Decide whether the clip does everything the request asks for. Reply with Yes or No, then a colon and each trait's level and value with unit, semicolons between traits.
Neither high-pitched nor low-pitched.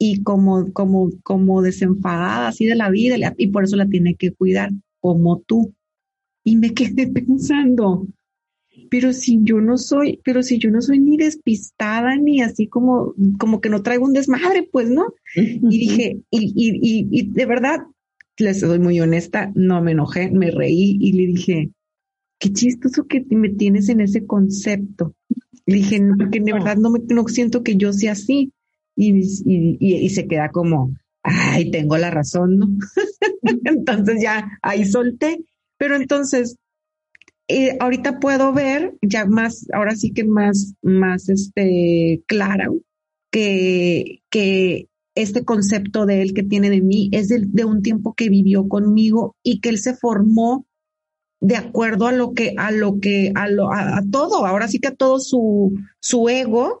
No: high, 215 Hz